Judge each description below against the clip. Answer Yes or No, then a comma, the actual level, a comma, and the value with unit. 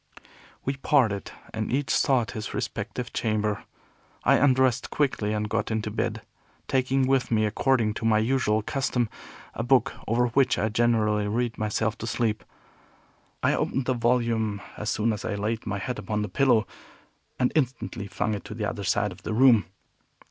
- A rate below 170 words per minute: No, average, 175 wpm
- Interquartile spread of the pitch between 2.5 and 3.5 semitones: Yes, average, 2.9 semitones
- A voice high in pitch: No, low, 115 Hz